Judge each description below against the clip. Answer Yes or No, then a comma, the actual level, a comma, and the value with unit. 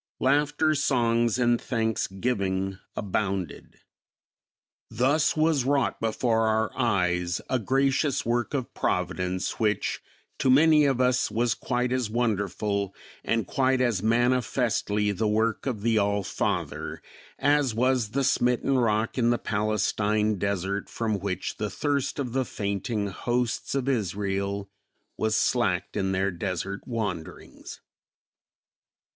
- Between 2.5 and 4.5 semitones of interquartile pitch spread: Yes, average, 4.1 semitones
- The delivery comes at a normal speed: No, slow, 125 wpm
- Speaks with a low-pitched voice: Yes, low, 115 Hz